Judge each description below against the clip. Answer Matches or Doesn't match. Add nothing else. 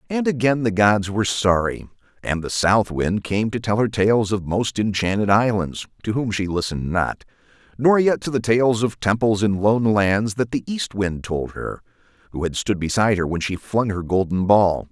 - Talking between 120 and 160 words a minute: Doesn't match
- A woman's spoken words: Doesn't match